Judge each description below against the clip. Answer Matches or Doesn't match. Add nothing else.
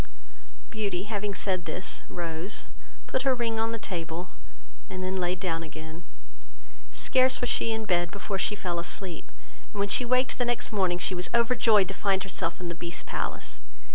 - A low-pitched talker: Doesn't match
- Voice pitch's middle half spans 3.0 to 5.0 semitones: Matches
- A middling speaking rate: Matches